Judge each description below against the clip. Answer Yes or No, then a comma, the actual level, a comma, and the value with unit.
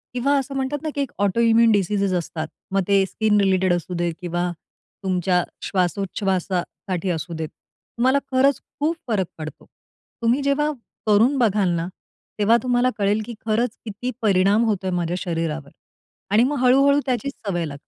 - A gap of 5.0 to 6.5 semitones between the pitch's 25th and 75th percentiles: Yes, wide, 5.4 semitones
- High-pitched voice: Yes, high, 205 Hz